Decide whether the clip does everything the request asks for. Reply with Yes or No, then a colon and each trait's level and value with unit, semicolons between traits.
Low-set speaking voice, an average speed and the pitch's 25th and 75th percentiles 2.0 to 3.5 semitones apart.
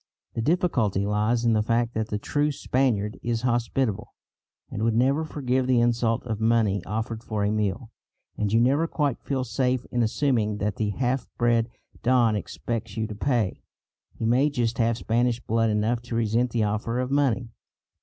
Yes: low, 115 Hz; average, 180 wpm; narrow, 2.5 semitones